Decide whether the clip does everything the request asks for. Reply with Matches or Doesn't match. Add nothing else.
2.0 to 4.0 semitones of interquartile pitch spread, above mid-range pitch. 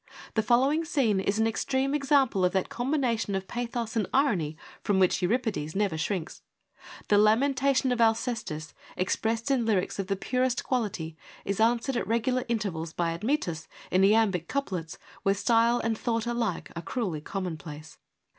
Doesn't match